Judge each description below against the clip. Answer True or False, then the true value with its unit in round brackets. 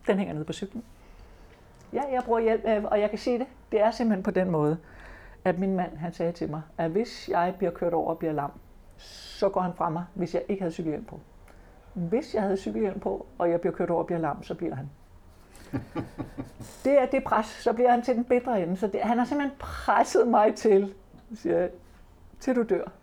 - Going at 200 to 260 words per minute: True (225 wpm)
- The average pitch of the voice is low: False (190 Hz)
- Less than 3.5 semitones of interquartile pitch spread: False (4.8 semitones)